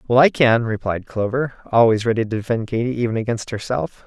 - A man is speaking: Yes, male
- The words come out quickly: No, average, 190 wpm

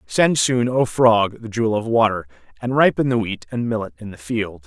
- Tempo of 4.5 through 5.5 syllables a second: Yes, 5.1 syllables/s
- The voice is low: Yes, low, 110 Hz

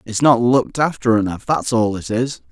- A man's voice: Yes, male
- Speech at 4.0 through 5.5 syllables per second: Yes, 5.2 syllables/s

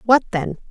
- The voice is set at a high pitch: Yes, high, 220 Hz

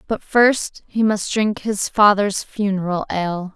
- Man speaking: No, female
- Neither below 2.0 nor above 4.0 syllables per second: Yes, 3.9 syllables/s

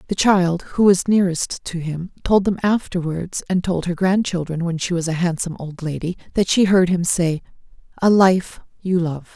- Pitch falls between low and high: Yes, medium, 180 Hz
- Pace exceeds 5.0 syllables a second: No, 4.9 syllables/s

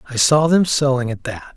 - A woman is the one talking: No, male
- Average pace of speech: No, fast, 230 wpm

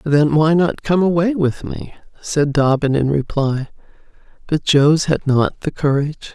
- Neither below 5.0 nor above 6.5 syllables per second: No, 4.4 syllables/s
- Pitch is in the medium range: Yes, medium, 150 Hz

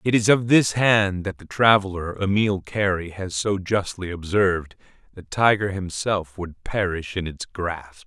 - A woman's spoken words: No, male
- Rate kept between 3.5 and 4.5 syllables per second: Yes, 4.4 syllables/s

